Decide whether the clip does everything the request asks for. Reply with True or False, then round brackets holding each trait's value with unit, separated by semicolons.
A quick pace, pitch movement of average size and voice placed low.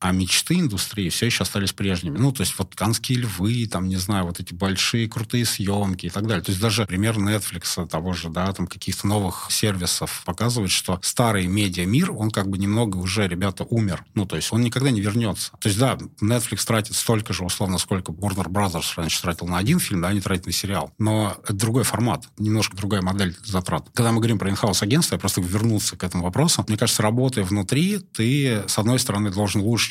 True (215 wpm; 3.5 semitones; 100 Hz)